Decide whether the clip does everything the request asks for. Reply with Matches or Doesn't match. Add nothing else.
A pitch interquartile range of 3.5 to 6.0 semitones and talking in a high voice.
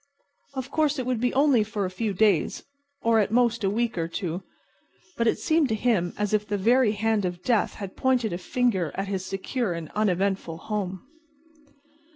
Matches